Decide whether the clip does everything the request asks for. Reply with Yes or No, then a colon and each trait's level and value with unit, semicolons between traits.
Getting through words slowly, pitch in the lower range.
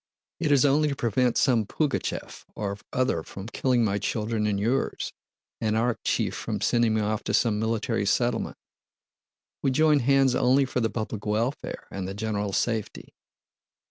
No: average, 160 wpm; low, 115 Hz